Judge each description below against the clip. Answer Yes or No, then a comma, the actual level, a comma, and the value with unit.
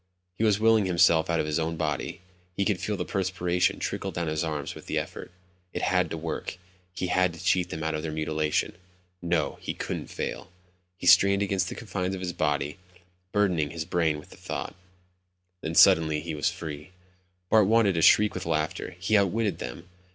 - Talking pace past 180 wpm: Yes, average, 195 wpm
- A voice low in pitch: Yes, very low, 85 Hz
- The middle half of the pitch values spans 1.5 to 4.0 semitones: Yes, average, 3.4 semitones